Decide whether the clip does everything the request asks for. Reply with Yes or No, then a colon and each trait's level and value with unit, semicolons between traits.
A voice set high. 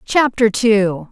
Yes: high, 215 Hz